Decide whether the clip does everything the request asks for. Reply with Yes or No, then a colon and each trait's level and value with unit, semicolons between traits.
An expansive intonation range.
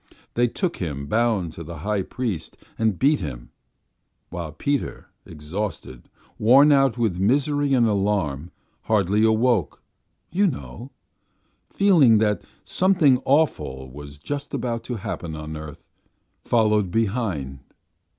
Yes: wide, 8.2 semitones